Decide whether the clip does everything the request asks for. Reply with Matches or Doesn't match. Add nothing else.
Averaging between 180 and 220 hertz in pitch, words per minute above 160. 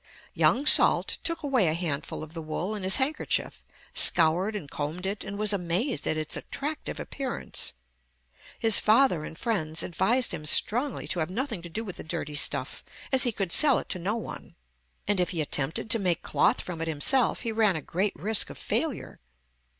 Matches